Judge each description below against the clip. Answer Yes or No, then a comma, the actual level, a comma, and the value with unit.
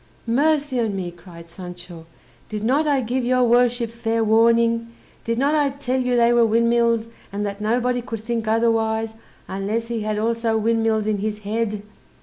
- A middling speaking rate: Yes, average, 170 wpm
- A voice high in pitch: Yes, high, 230 Hz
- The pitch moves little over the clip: Yes, narrow, 2.0 semitones